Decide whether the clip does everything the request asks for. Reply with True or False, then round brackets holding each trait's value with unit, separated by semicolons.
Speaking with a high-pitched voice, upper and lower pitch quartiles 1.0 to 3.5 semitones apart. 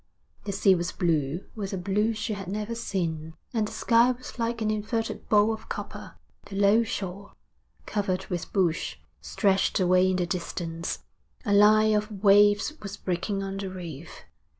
True (200 Hz; 2.8 semitones)